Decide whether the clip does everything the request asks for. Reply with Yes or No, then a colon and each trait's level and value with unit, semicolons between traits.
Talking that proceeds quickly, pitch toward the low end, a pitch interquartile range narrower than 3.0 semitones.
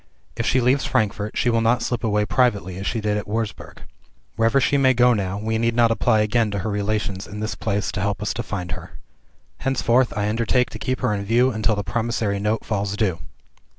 Yes: fast, 220 wpm; low, 110 Hz; narrow, 2.5 semitones